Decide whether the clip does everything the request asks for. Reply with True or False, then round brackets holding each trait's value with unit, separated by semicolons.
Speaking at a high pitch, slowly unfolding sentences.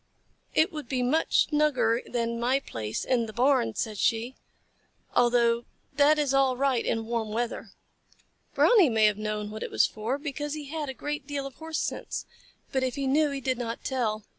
False (255 Hz; 190 wpm)